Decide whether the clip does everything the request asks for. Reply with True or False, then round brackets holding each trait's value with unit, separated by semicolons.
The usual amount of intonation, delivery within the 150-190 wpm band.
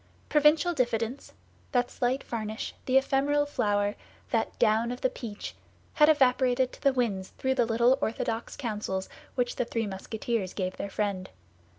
True (3.6 semitones; 155 wpm)